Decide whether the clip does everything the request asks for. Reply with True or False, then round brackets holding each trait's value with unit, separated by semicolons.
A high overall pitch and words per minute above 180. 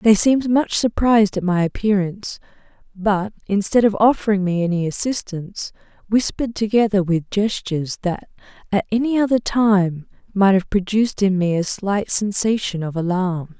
False (200 Hz; 145 wpm)